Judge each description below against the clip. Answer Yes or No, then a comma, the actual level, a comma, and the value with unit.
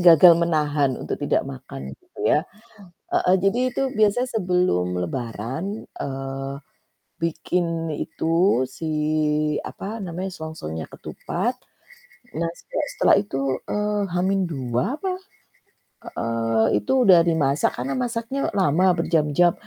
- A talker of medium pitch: Yes, medium, 165 Hz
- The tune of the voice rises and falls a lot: Yes, wide, 6.1 semitones